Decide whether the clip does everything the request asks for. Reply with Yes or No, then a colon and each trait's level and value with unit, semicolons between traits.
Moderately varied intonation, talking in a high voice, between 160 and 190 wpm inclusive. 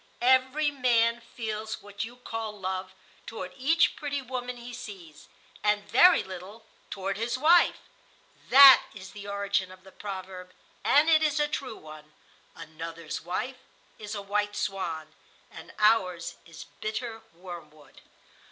No: average, 4.9 semitones; high, 210 Hz; slow, 135 wpm